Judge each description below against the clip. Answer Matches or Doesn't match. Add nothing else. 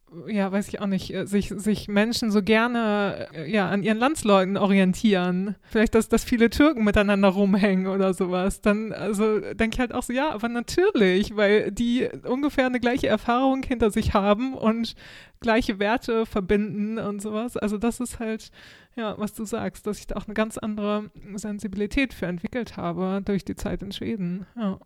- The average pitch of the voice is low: Doesn't match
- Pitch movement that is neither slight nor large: Doesn't match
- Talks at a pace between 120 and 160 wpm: Doesn't match